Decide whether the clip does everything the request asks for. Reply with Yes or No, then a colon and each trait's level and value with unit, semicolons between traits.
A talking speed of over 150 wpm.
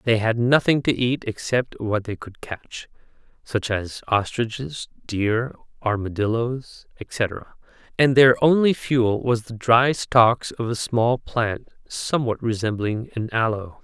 No: average, 140 wpm